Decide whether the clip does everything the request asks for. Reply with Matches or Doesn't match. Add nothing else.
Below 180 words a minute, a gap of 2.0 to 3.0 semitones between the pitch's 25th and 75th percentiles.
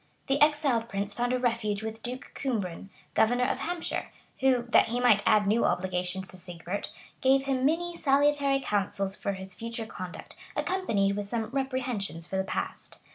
Doesn't match